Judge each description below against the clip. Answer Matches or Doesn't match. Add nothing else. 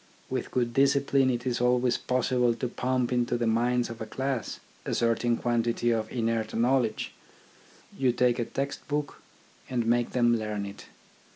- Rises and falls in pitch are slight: Matches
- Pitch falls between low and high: Doesn't match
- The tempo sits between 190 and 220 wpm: Doesn't match